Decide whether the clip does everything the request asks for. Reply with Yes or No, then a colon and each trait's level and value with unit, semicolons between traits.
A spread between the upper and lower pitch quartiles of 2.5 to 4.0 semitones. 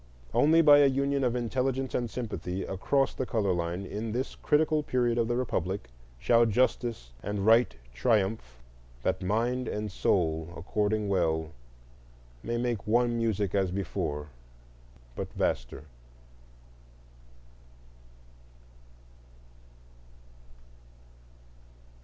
No: average, 4.8 semitones